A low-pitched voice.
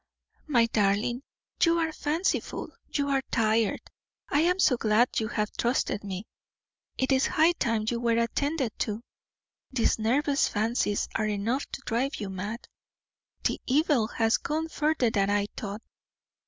No: high, 235 Hz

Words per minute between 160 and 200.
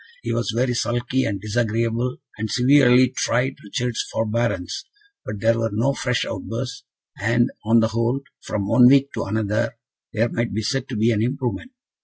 Yes: average, 170 wpm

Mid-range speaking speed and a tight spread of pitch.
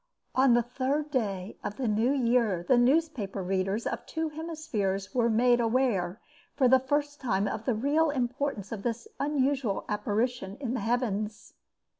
No: average, 160 wpm; average, 4.6 semitones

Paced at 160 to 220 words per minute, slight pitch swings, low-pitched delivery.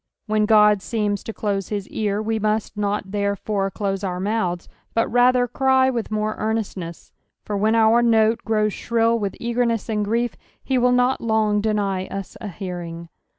No: average, 170 wpm; narrow, 2.2 semitones; high, 215 Hz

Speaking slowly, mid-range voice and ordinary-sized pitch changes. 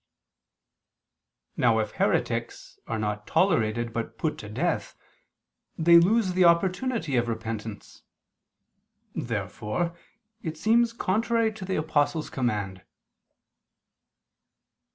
No: slow, 95 wpm; medium, 155 Hz; wide, 8.8 semitones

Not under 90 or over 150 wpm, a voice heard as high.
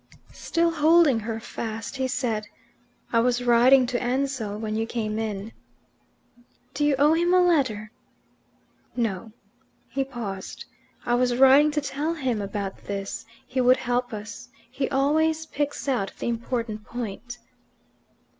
Yes: average, 140 wpm; high, 245 Hz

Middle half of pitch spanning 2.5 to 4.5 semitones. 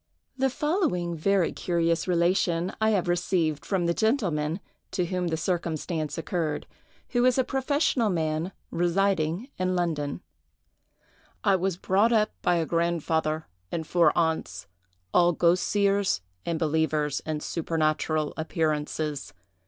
Yes: average, 3.3 semitones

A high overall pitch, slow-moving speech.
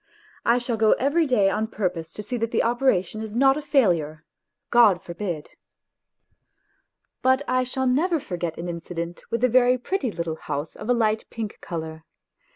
No: high, 220 Hz; average, 170 wpm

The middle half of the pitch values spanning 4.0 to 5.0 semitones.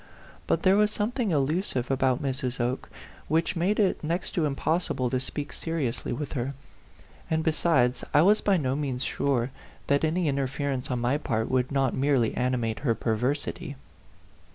Yes: average, 4.3 semitones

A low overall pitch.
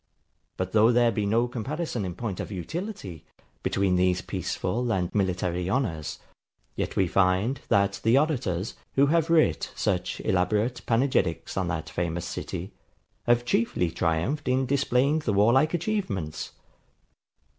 Yes: low, 110 Hz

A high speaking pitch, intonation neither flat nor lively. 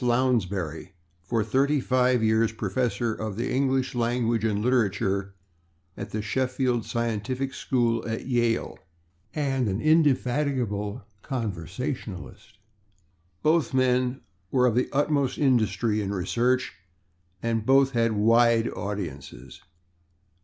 No: low, 120 Hz; average, 3.5 semitones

